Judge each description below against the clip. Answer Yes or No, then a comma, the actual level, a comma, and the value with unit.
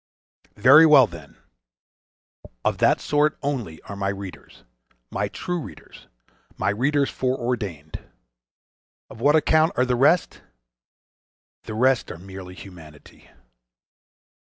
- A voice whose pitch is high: No, low, 115 Hz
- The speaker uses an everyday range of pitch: No, wide, 7.5 semitones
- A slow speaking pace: Yes, slow, 110 wpm